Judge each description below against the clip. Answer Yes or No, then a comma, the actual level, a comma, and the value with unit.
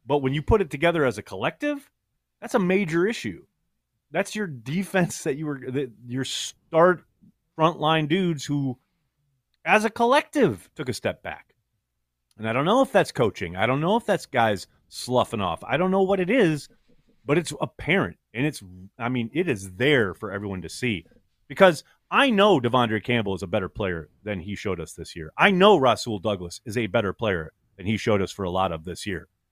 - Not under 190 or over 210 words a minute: Yes, fast, 205 wpm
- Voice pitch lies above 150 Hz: No, low, 135 Hz